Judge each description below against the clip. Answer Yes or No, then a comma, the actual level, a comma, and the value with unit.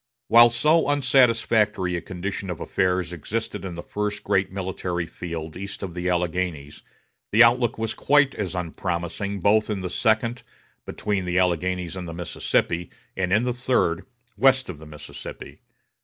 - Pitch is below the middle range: Yes, very low, 95 Hz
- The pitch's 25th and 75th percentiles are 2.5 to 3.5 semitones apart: No, average, 4.3 semitones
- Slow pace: No, average, 155 wpm